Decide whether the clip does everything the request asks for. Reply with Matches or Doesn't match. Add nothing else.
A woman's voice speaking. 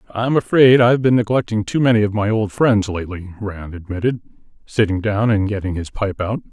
Doesn't match